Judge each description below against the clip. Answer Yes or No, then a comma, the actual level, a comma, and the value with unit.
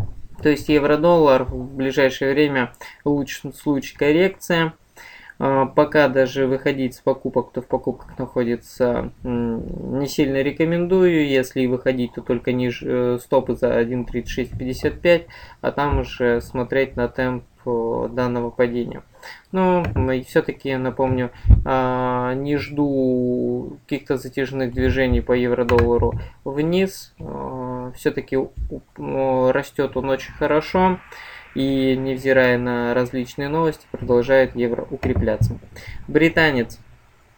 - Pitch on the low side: Yes, low, 130 Hz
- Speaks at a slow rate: Yes, slow, 100 wpm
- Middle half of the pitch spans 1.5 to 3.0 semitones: Yes, narrow, 2.4 semitones